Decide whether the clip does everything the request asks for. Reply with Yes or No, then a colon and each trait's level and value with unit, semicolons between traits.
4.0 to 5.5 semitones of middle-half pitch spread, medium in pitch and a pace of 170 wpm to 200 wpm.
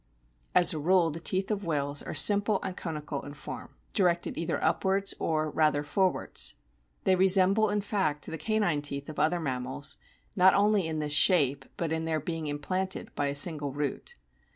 Yes: average, 4.4 semitones; medium, 160 Hz; average, 175 wpm